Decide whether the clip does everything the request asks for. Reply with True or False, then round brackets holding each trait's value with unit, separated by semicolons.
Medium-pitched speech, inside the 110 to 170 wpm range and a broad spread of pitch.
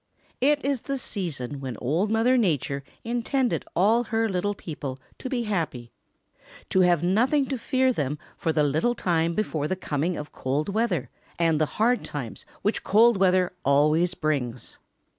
True (180 Hz; 160 wpm; 7.4 semitones)